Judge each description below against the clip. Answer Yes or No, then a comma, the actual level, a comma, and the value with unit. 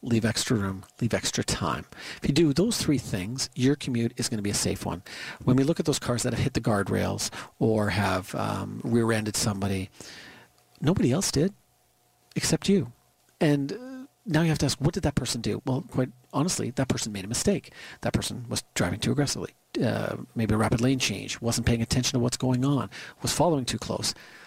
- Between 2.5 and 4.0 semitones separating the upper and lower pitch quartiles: No, average, 4.4 semitones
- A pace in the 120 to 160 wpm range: No, fast, 205 wpm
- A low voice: Yes, low, 120 Hz